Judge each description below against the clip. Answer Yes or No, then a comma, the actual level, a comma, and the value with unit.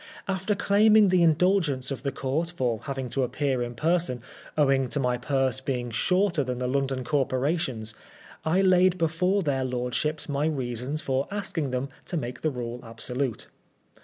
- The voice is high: No, medium, 140 Hz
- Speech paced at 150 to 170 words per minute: Yes, average, 160 wpm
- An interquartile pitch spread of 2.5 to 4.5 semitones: No, average, 5.0 semitones